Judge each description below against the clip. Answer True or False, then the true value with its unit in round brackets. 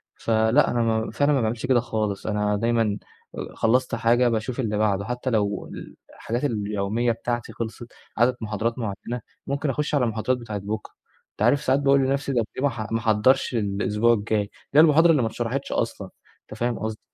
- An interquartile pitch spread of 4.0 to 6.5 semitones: False (3.0 semitones)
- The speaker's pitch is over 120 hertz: False (115 Hz)